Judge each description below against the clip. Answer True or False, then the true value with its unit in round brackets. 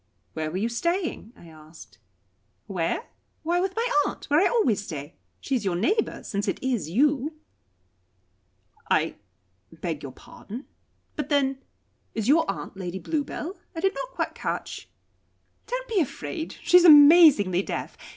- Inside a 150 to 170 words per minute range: True (155 wpm)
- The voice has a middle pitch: False (265 Hz)